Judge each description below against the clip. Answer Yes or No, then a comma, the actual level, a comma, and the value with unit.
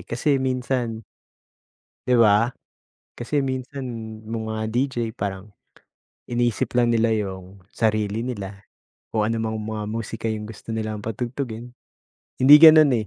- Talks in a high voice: No, low, 115 Hz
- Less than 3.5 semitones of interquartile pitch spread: Yes, average, 2.7 semitones